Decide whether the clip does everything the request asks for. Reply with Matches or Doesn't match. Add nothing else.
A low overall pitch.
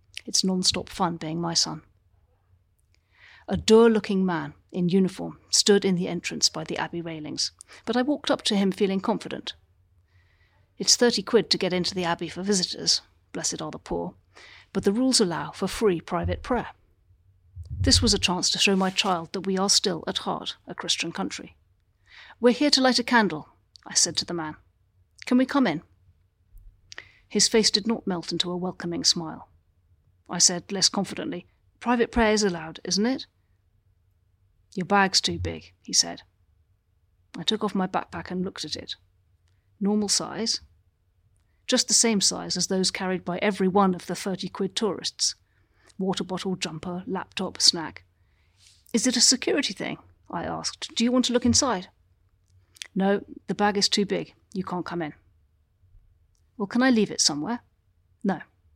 Doesn't match